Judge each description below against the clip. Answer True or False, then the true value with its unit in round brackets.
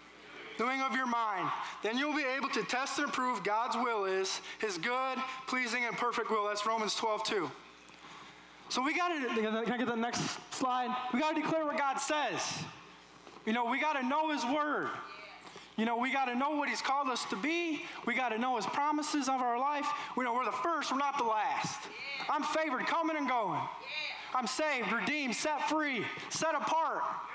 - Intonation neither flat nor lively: True (4.0 semitones)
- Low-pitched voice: False (260 Hz)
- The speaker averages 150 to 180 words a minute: False (200 wpm)